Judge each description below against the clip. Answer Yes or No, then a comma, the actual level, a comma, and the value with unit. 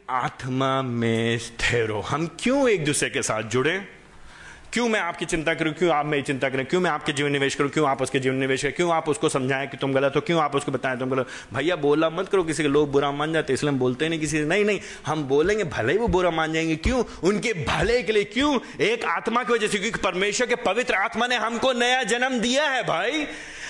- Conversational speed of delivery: No, fast, 235 wpm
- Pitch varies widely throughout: Yes, wide, 7.3 semitones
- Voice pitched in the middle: Yes, medium, 160 Hz